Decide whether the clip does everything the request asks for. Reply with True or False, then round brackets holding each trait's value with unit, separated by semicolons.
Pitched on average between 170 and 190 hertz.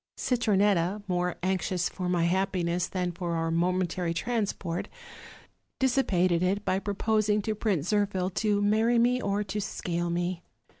True (185 Hz)